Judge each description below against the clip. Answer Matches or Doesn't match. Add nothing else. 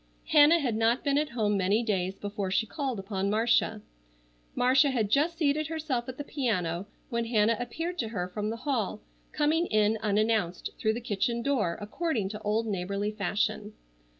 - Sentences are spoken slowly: Doesn't match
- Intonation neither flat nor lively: Matches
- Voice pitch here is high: Matches